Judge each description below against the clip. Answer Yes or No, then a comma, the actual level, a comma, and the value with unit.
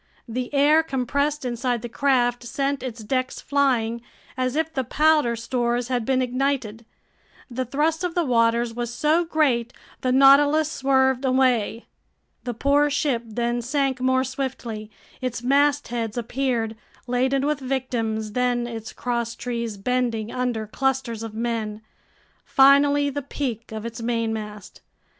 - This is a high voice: Yes, very high, 250 Hz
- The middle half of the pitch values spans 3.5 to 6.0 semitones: No, average, 2.8 semitones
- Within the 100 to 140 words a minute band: Yes, slow, 135 wpm